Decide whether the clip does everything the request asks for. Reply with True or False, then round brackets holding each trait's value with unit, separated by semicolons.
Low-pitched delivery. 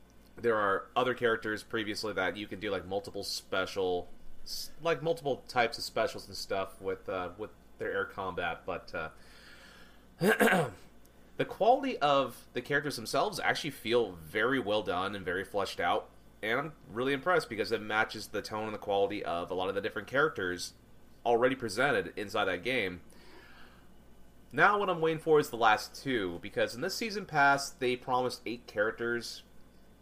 True (120 Hz)